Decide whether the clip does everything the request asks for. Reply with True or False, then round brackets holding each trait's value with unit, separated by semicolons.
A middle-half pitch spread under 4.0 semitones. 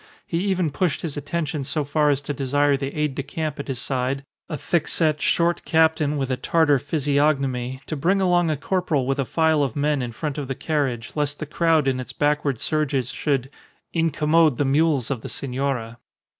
True (2.7 semitones)